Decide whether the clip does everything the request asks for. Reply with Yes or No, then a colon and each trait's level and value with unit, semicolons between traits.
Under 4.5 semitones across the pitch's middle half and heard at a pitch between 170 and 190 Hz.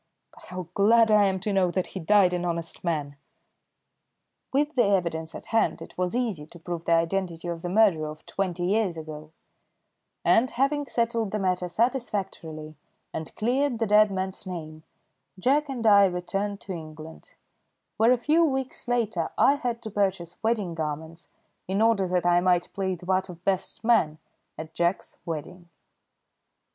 No: average, 4.8 semitones; medium, 185 Hz